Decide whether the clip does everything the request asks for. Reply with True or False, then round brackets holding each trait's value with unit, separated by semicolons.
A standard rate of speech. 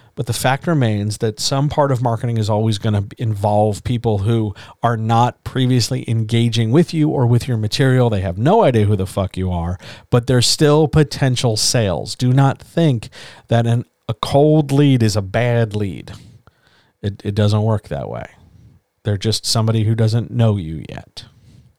True (180 wpm)